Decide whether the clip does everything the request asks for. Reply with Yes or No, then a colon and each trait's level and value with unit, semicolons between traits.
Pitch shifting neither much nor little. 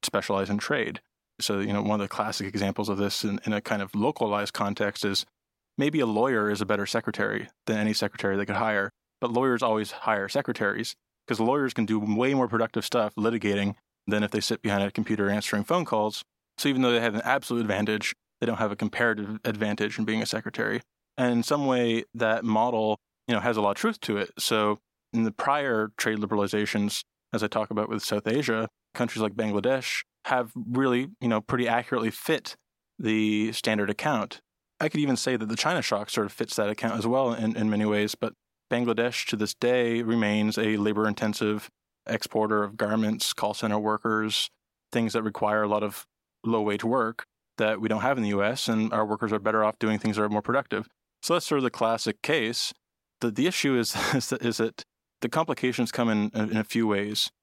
No: narrow, 2.0 semitones